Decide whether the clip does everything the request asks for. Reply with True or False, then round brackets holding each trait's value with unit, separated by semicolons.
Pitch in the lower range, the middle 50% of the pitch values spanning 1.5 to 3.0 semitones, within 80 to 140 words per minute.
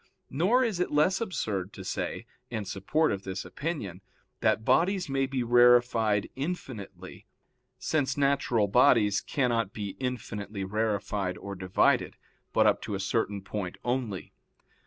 False (115 Hz; 5.6 semitones; 135 wpm)